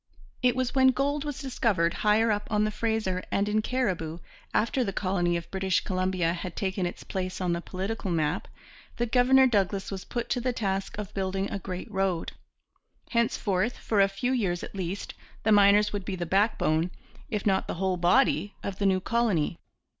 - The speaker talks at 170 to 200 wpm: Yes, average, 190 wpm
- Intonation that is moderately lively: Yes, average, 3.6 semitones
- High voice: Yes, high, 195 Hz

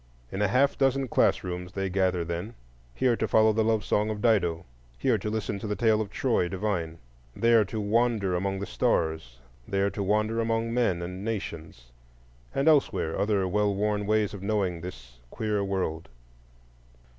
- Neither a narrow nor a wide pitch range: Yes, average, 3.8 semitones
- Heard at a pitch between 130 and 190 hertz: No, low, 100 Hz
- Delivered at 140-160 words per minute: No, average, 170 wpm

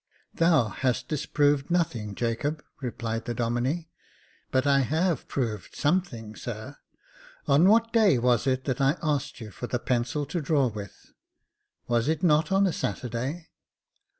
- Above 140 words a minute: Yes, average, 150 wpm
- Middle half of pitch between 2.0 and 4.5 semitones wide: No, average, 4.9 semitones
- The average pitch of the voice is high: No, low, 135 Hz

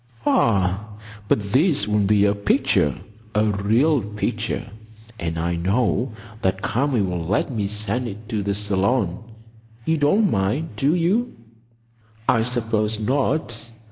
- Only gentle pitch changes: No, average, 4.2 semitones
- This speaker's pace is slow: Yes, slow, 130 wpm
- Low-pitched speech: Yes, low, 105 Hz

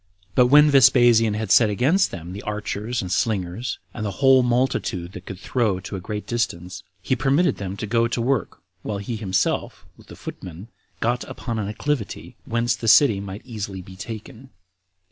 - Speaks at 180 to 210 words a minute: Yes, average, 185 wpm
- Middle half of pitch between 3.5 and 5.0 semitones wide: Yes, average, 4.0 semitones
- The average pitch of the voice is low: Yes, low, 110 Hz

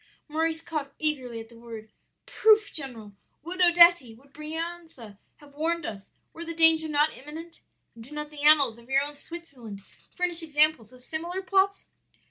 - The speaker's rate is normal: Yes, average, 165 wpm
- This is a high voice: Yes, very high, 300 Hz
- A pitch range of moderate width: Yes, average, 4.7 semitones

